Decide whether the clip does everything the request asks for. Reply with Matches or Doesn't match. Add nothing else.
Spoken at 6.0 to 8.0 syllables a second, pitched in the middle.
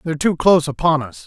Matches